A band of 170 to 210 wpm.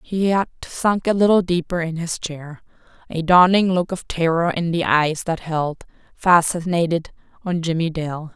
No: average, 160 wpm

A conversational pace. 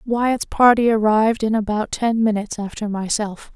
Yes: average, 150 wpm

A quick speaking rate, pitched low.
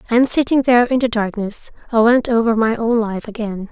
No: fast, 210 wpm; high, 230 Hz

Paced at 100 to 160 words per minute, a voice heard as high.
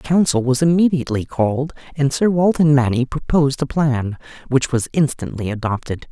No: average, 155 wpm; medium, 140 Hz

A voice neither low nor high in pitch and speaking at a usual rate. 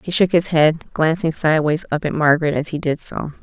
No: medium, 160 Hz; fast, 230 wpm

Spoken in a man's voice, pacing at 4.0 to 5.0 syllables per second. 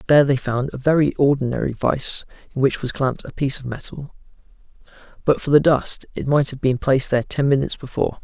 No: male; 6.5 syllables/s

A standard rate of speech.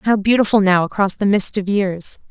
No: fast, 210 wpm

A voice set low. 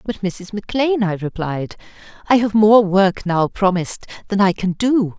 No: high, 200 Hz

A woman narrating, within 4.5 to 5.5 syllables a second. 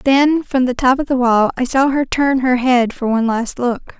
Yes: female; 4.8 syllables/s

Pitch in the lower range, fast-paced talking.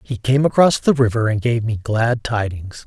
Yes: low, 115 Hz; fast, 210 wpm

